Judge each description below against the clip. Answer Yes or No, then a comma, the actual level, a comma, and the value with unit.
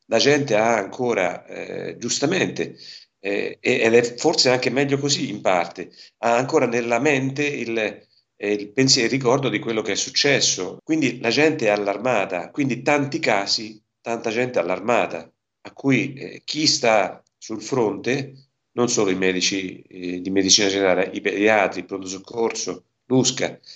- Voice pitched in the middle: No, low, 115 Hz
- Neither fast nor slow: Yes, average, 155 wpm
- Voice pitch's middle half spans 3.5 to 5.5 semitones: Yes, average, 4.7 semitones